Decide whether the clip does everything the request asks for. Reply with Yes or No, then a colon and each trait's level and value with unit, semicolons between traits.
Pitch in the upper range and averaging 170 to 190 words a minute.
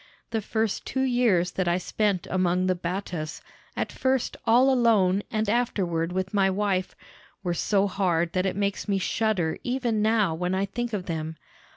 Yes: high, 195 Hz; average, 175 wpm